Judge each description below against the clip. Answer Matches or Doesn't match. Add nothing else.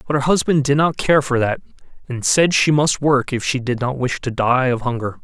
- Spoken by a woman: Doesn't match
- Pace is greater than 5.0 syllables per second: Matches